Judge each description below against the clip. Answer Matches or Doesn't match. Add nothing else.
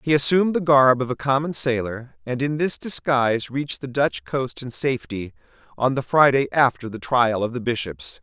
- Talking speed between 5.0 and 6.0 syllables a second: Matches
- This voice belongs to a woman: Doesn't match